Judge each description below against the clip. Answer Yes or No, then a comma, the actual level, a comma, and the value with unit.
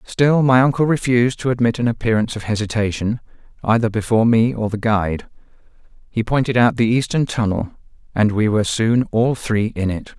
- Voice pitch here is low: Yes, low, 115 Hz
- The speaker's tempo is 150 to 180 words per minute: Yes, average, 175 wpm